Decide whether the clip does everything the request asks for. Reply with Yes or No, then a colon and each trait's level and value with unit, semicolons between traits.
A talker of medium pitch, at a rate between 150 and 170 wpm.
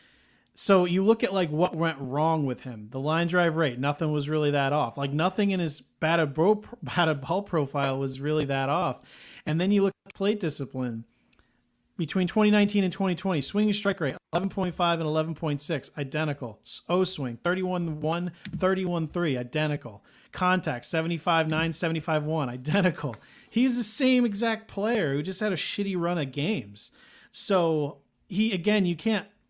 Yes: medium, 165 Hz; average, 165 wpm